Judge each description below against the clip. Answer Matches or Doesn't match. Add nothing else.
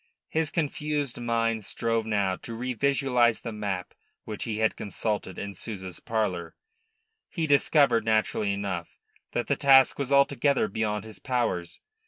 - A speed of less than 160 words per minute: Matches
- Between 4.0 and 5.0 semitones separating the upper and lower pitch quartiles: Matches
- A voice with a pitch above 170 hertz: Doesn't match